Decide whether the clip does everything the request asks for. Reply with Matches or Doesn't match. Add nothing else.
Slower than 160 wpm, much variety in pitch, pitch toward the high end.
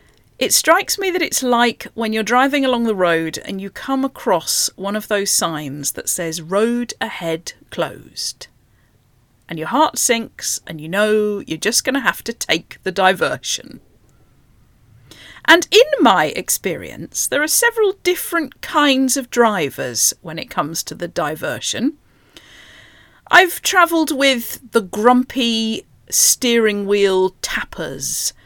Matches